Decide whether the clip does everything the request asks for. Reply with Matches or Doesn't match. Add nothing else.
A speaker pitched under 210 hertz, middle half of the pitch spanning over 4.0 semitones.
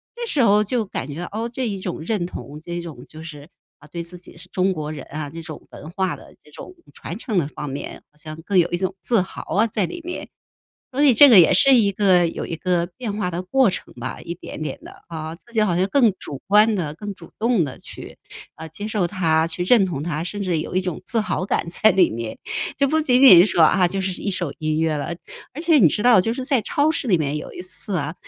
Matches